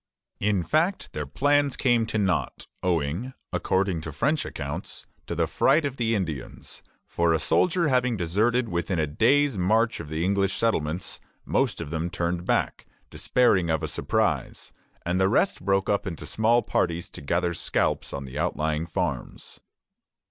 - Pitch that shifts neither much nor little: No, wide, 6.1 semitones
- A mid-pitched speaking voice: No, very low, 95 Hz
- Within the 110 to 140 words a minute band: No, average, 160 wpm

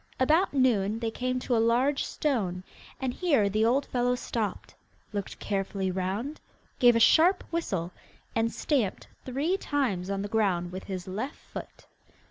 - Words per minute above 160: No, average, 155 wpm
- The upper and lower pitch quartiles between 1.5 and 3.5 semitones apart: No, average, 5.2 semitones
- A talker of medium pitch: No, high, 230 Hz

